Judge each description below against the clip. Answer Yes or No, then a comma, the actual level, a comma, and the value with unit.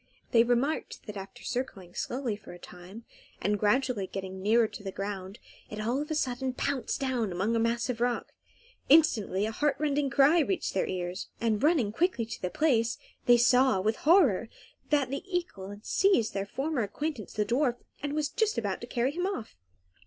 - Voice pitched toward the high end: Yes, high, 240 Hz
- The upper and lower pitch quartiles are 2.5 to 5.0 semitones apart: No, wide, 5.4 semitones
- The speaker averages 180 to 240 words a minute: Yes, average, 190 wpm